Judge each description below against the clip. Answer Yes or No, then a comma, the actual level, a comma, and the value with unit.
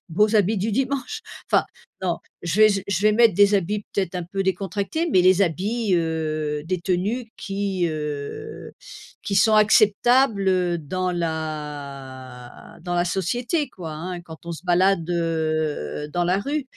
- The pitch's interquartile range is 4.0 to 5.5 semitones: Yes, average, 4.3 semitones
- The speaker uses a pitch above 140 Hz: Yes, medium, 185 Hz